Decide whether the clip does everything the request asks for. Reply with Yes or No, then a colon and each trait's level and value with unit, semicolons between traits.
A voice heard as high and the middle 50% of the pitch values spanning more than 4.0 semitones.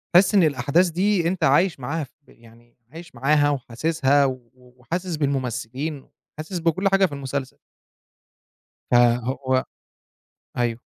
No: medium, 140 Hz; average, 4.8 semitones